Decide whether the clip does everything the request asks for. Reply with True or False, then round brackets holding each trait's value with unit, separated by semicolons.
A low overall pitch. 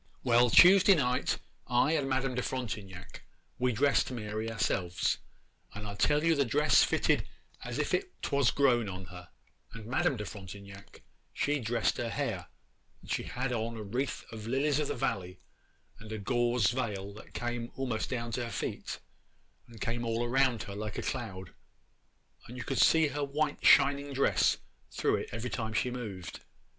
True (120 Hz)